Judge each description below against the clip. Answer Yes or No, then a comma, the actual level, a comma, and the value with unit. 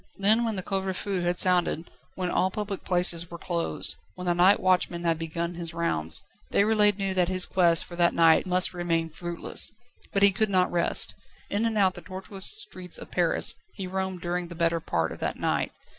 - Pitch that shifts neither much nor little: No, narrow, 2.1 semitones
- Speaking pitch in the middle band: Yes, medium, 180 Hz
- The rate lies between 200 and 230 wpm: Yes, fast, 205 wpm